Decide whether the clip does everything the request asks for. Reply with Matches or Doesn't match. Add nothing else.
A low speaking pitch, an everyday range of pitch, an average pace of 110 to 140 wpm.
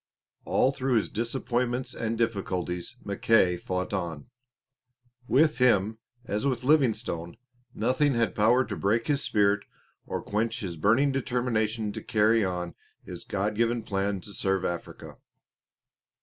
Matches